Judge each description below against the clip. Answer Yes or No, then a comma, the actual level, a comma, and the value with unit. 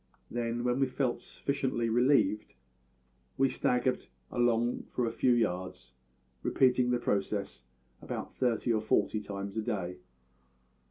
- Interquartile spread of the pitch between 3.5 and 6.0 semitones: No, average, 2.7 semitones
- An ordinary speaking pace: No, slow, 125 wpm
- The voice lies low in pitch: Yes, low, 120 Hz